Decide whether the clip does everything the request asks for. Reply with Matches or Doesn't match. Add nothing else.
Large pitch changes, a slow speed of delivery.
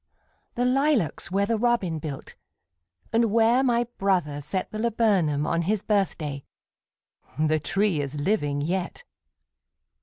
Matches